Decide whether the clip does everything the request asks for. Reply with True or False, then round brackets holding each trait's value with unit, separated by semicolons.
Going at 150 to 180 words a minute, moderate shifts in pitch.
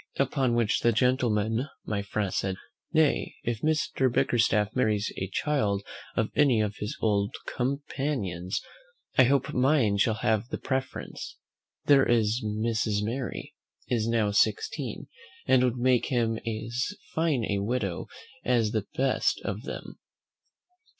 False (135 wpm; 3.7 semitones)